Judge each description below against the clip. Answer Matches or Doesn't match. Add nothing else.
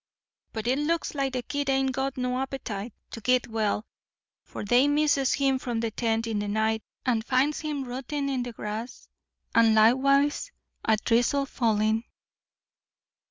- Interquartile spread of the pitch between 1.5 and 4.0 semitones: Matches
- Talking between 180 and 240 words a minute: Doesn't match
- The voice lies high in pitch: Matches